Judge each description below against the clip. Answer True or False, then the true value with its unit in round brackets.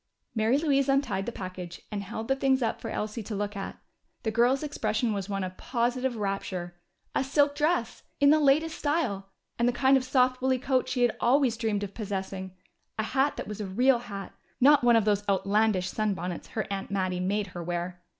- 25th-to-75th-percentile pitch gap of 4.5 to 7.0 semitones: True (5.1 semitones)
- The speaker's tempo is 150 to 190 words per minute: False (205 wpm)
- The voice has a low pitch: False (220 Hz)